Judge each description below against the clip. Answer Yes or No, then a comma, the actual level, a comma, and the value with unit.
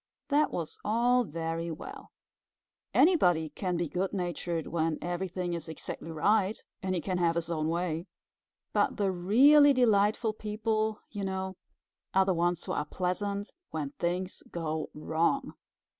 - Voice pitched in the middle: Yes, medium, 180 Hz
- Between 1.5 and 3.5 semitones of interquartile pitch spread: No, average, 3.9 semitones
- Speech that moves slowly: No, average, 145 wpm